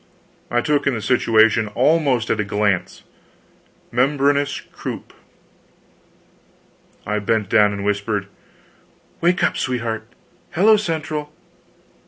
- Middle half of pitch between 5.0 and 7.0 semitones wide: Yes, wide, 5.5 semitones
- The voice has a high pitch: No, low, 120 Hz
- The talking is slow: Yes, slow, 105 wpm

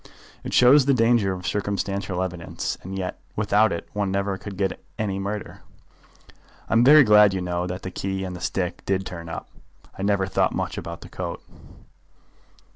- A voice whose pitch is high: No, very low, 95 Hz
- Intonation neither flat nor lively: No, narrow, 2.1 semitones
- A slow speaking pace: No, average, 185 wpm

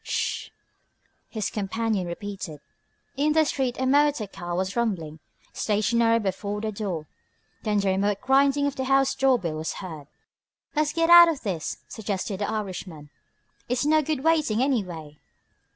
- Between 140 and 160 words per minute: Yes, average, 150 wpm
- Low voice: No, high, 215 Hz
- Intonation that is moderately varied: No, wide, 6.2 semitones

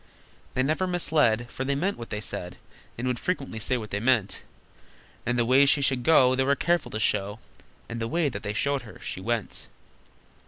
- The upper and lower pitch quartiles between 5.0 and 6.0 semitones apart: No, average, 4.1 semitones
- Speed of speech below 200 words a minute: No, fast, 205 wpm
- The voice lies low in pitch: Yes, low, 125 Hz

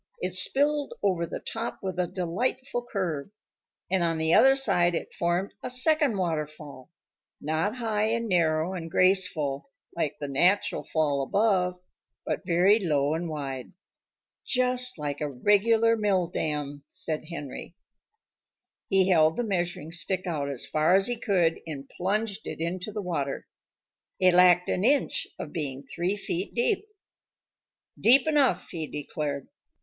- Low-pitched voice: No, medium, 180 Hz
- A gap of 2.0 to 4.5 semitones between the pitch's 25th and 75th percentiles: No, average, 5.1 semitones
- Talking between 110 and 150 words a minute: Yes, average, 145 wpm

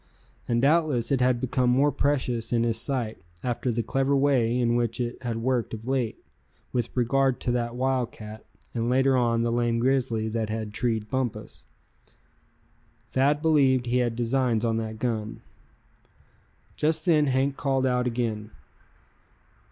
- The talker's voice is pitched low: Yes, low, 125 Hz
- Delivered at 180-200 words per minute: No, average, 150 wpm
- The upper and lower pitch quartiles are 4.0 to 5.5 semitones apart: No, narrow, 2.4 semitones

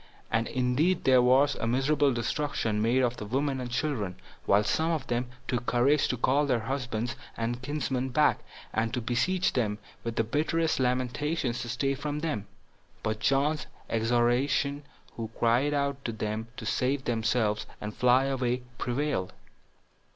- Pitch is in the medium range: No, low, 125 Hz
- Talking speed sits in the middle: Yes, average, 160 wpm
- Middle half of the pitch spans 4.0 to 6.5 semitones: No, average, 3.3 semitones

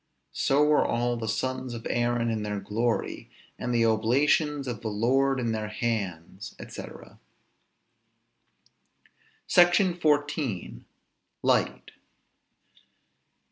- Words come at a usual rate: No, slow, 100 wpm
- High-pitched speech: No, low, 120 Hz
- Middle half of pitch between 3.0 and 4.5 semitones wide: Yes, average, 3.7 semitones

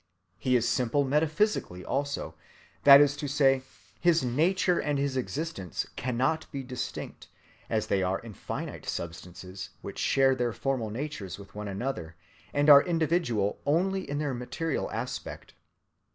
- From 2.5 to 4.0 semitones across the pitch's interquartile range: No, average, 5.1 semitones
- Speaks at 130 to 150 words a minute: Yes, average, 145 wpm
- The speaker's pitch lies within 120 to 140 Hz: Yes, low, 135 Hz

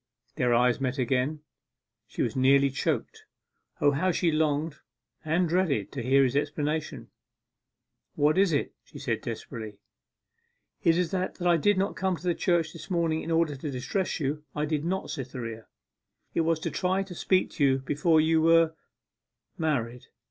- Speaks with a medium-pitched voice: Yes, medium, 155 Hz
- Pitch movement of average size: Yes, average, 3.8 semitones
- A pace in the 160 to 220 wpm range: Yes, average, 170 wpm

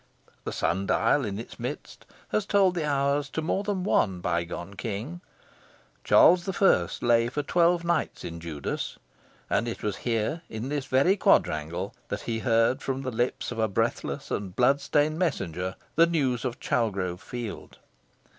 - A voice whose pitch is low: Yes, low, 120 Hz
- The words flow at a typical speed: Yes, average, 165 wpm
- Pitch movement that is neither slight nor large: No, wide, 7.1 semitones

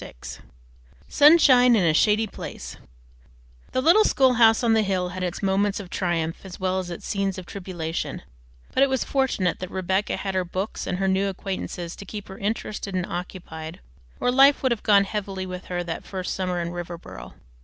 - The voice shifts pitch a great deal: No, average, 3.3 semitones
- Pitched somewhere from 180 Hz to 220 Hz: Yes, high, 190 Hz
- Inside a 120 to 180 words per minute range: No, average, 190 wpm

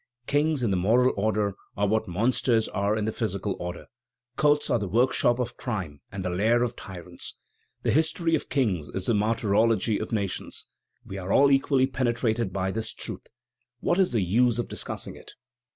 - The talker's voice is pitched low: Yes, low, 110 Hz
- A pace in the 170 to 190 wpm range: Yes, average, 185 wpm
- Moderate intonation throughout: Yes, average, 4.2 semitones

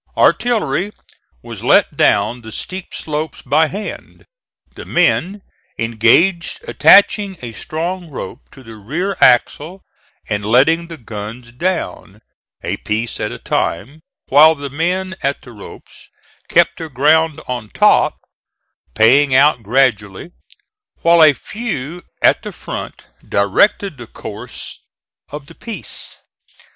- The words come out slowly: Yes, slow, 125 wpm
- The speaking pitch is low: No, medium, 145 Hz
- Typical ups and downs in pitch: No, wide, 6.7 semitones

